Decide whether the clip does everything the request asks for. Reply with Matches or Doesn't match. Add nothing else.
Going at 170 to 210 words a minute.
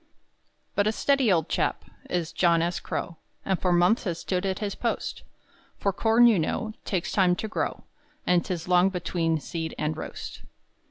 Matches